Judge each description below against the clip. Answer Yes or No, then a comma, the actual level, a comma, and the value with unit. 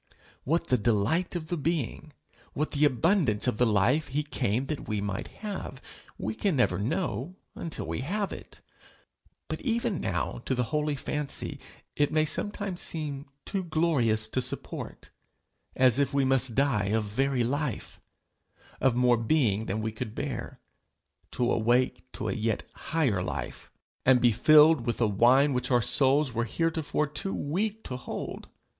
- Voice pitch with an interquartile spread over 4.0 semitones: Yes, average, 4.9 semitones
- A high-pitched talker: No, low, 135 Hz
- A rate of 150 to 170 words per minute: Yes, average, 165 wpm